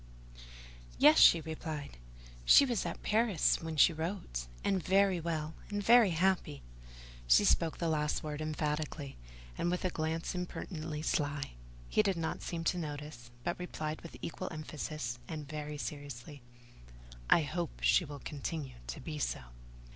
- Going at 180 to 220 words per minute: No, average, 155 wpm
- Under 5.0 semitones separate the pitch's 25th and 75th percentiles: Yes, average, 3.0 semitones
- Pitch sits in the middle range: Yes, medium, 155 Hz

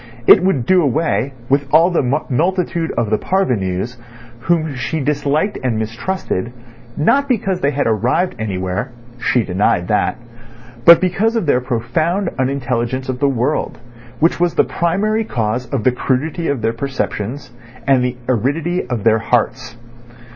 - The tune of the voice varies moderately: No, wide, 6.0 semitones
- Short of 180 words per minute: Yes, average, 150 wpm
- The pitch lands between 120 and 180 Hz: Yes, low, 135 Hz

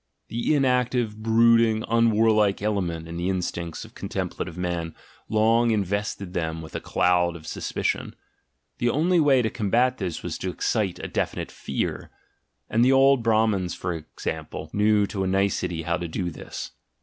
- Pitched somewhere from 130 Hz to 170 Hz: No, low, 105 Hz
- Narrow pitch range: No, average, 4.8 semitones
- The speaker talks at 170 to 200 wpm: No, average, 160 wpm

